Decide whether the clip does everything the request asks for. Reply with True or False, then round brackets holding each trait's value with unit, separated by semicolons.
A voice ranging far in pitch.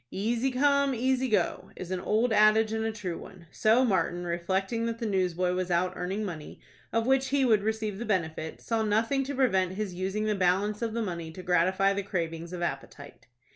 False (4.1 semitones)